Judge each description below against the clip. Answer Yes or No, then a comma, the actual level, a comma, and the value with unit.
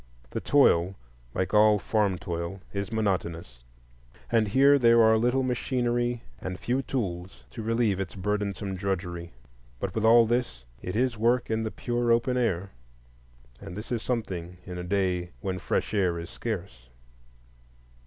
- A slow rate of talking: No, average, 155 wpm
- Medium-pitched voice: No, low, 105 Hz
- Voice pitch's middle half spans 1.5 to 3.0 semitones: No, average, 4.5 semitones